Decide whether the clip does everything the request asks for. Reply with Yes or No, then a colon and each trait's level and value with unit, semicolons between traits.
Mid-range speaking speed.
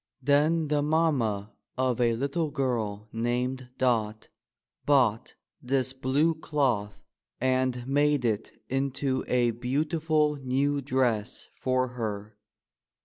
No: slow, 105 wpm